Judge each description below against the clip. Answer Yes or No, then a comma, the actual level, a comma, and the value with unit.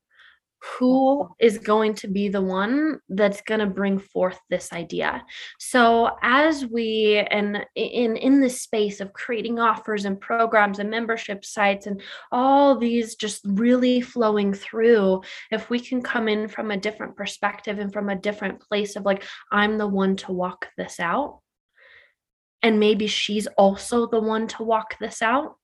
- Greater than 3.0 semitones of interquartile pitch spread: No, narrow, 2.4 semitones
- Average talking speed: Yes, average, 165 wpm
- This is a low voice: No, high, 215 Hz